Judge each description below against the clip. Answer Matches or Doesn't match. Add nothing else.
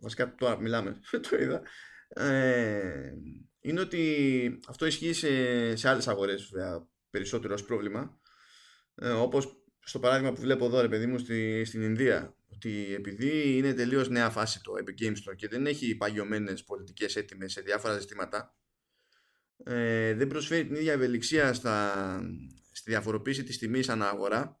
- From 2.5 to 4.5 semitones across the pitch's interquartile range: Matches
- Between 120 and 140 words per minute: Doesn't match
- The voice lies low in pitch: Matches